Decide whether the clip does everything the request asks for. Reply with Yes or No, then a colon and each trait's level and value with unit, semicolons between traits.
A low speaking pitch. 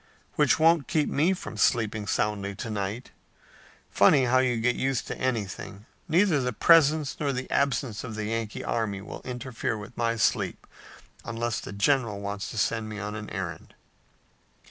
Yes: low, 115 Hz